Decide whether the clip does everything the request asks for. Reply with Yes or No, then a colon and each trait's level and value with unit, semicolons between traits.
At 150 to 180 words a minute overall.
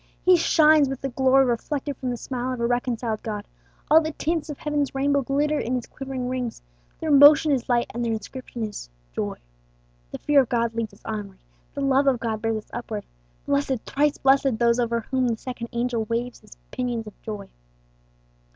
No: average, 195 wpm